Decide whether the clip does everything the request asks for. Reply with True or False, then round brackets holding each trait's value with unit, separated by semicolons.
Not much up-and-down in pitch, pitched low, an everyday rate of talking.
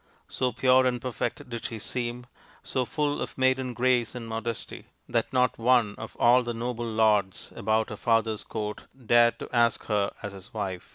True (2.3 semitones; 120 Hz; 180 wpm)